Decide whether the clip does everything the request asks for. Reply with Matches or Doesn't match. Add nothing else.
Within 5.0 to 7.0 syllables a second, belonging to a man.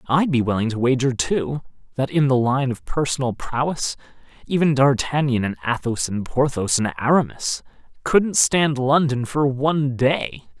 Doesn't match